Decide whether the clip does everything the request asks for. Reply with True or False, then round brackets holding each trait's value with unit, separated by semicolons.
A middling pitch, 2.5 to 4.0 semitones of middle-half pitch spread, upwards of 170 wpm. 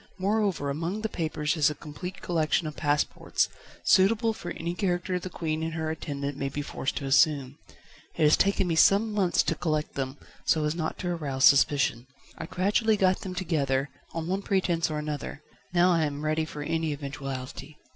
True (160 Hz; 3.7 semitones; 185 wpm)